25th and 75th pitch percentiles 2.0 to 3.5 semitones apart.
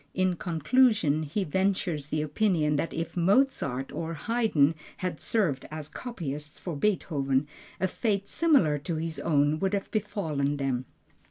No: average, 5.2 semitones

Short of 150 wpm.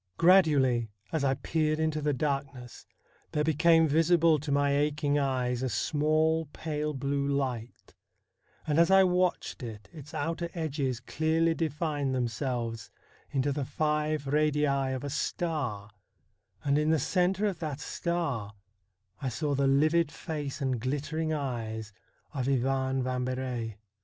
Yes: slow, 135 wpm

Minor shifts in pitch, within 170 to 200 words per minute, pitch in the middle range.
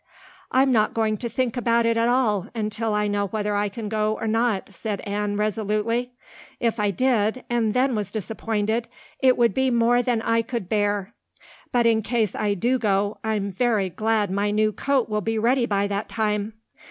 No: narrow, 2.2 semitones; average, 190 wpm; high, 220 Hz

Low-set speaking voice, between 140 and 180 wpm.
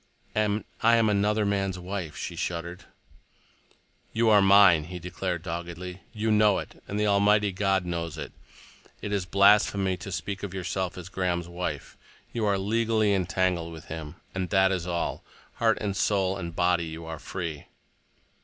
Yes: very low, 95 Hz; average, 165 wpm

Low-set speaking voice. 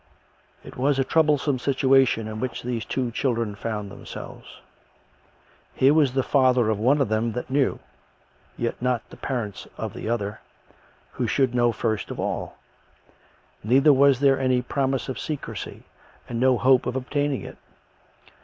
Yes: low, 125 Hz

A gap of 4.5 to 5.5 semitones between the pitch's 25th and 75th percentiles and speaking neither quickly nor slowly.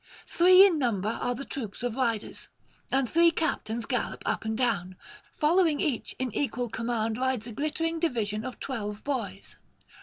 Yes: average, 4.9 semitones; average, 160 wpm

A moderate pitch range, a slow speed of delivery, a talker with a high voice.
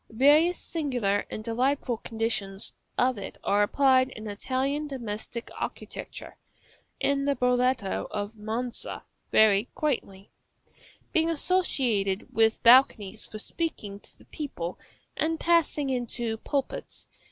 Yes: average, 4.8 semitones; slow, 115 wpm; high, 245 Hz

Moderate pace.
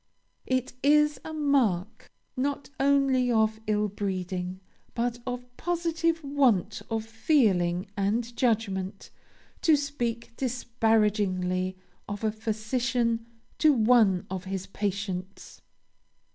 No: slow, 105 wpm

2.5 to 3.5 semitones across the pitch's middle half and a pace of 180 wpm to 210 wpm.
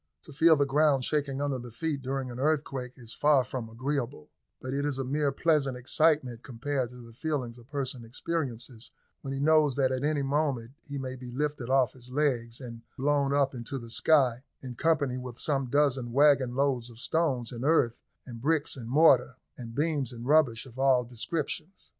Yes: average, 3.0 semitones; average, 195 wpm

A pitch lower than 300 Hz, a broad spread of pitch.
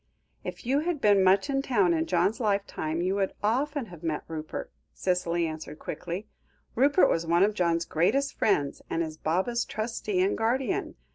Yes: high, 190 Hz; wide, 5.9 semitones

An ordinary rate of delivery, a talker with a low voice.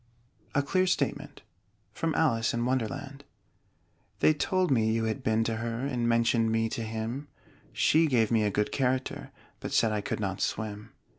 Yes: average, 170 wpm; low, 115 Hz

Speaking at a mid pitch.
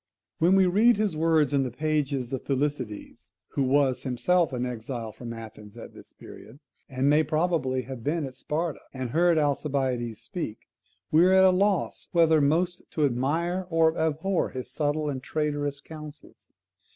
Yes: medium, 145 Hz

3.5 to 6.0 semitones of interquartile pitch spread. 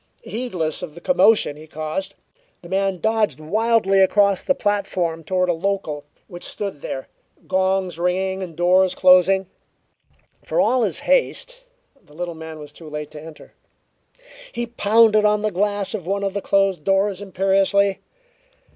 No: average, 3.1 semitones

